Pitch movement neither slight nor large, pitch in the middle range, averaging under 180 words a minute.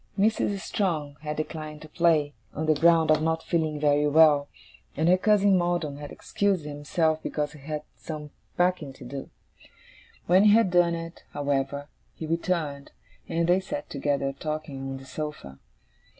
Yes: average, 3.0 semitones; medium, 155 Hz; average, 165 wpm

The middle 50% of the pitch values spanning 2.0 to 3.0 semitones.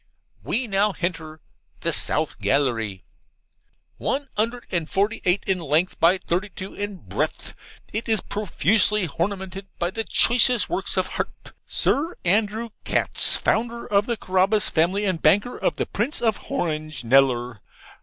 No: average, 4.7 semitones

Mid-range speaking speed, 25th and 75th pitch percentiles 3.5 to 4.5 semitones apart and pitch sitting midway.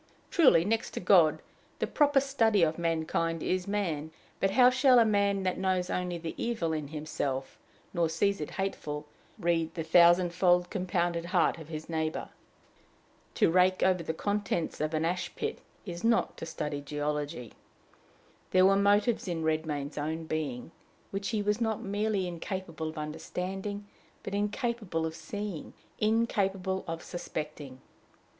Yes: average, 150 wpm; average, 4.1 semitones; medium, 175 Hz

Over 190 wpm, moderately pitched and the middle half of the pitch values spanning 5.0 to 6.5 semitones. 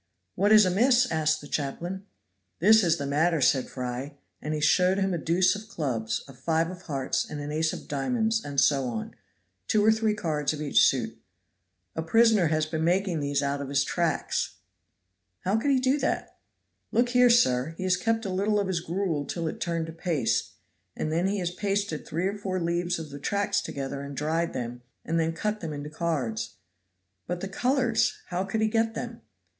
Yes: fast, 205 wpm; medium, 170 Hz; wide, 5.4 semitones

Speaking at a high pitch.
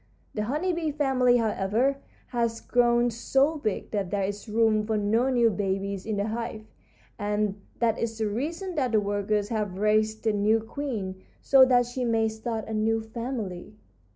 Yes: high, 220 Hz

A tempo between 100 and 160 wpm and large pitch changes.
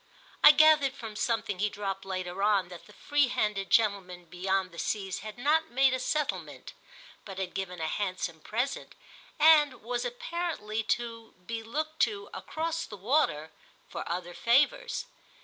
Yes: average, 155 wpm; wide, 6.5 semitones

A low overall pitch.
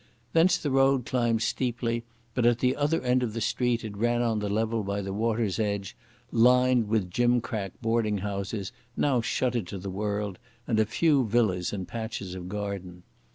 Yes: low, 115 Hz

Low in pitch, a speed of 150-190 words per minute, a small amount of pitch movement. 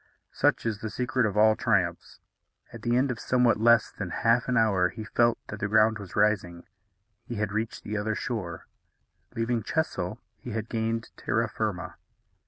Yes: low, 110 Hz; average, 180 wpm; narrow, 2.3 semitones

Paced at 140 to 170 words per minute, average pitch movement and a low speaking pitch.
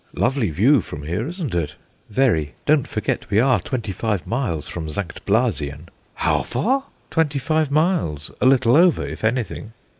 No: average, 160 wpm; wide, 8.3 semitones; low, 115 Hz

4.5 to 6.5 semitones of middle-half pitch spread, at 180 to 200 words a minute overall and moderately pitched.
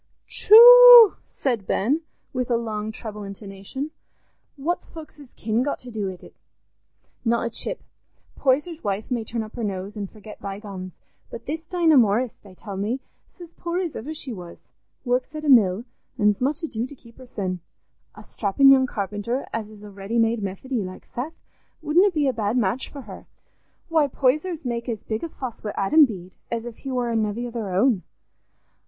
No: average, 5.2 semitones; average, 185 wpm; high, 235 Hz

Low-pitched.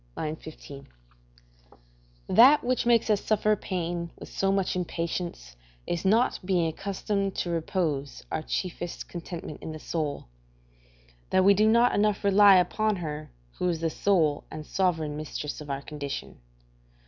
No: medium, 175 Hz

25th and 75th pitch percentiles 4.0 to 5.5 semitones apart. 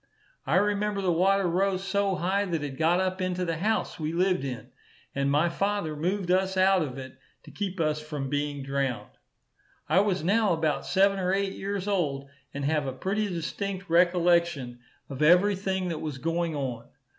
Yes: average, 4.3 semitones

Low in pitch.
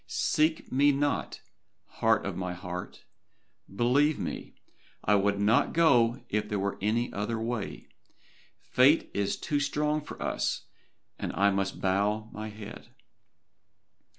Yes: low, 110 Hz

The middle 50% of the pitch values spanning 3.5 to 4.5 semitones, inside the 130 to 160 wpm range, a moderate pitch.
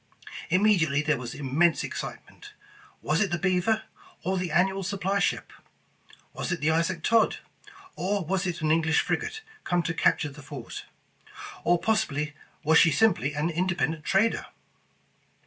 Yes: average, 3.9 semitones; average, 145 wpm; medium, 170 Hz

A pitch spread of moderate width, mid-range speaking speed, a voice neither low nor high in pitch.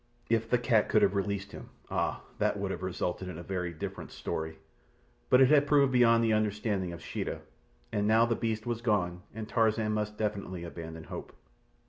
No: average, 3.9 semitones; average, 190 wpm; low, 105 Hz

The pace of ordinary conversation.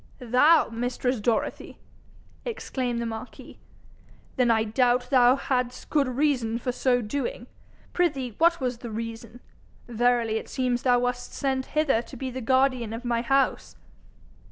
Yes: average, 150 wpm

